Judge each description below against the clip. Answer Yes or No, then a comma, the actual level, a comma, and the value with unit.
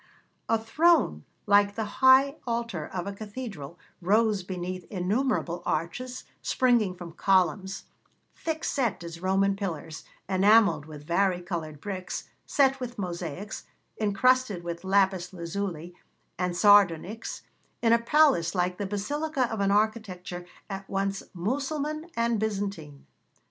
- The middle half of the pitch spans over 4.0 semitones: Yes, average, 4.5 semitones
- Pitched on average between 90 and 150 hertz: No, high, 200 Hz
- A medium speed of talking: No, slow, 125 wpm